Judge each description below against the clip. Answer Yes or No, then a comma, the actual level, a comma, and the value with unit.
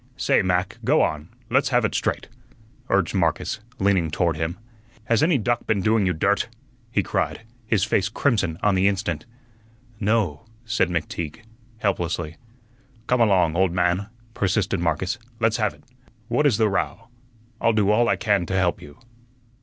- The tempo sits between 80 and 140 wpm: No, average, 160 wpm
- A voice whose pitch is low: Yes, low, 100 Hz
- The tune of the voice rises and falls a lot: No, average, 4.3 semitones